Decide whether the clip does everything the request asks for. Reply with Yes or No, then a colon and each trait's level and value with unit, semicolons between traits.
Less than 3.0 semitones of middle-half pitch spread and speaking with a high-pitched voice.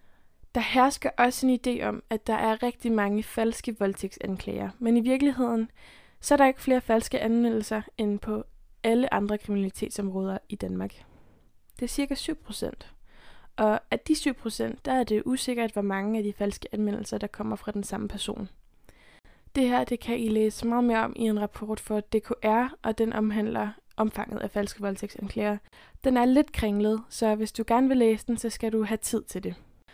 Yes: narrow, 2.6 semitones; high, 220 Hz